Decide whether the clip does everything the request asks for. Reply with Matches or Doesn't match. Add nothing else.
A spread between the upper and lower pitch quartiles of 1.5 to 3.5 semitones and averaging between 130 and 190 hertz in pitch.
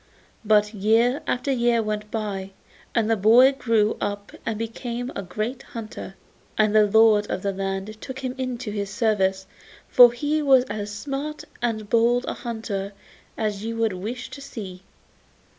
Doesn't match